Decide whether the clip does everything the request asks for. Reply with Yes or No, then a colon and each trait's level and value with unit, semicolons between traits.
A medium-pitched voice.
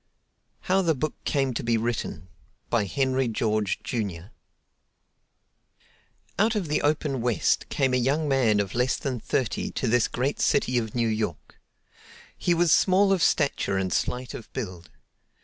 No: low, 125 Hz